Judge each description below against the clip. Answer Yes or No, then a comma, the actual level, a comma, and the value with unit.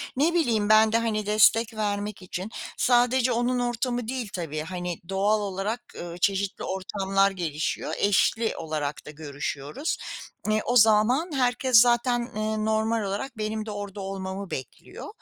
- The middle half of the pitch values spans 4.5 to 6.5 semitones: No, average, 3.8 semitones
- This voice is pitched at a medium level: No, high, 215 Hz